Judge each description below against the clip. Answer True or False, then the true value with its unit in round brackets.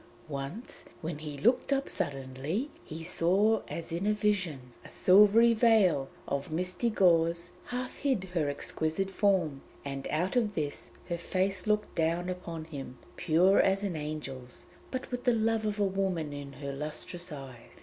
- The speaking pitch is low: False (175 Hz)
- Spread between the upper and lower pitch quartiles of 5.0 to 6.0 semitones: True (5.5 semitones)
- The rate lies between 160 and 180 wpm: True (165 wpm)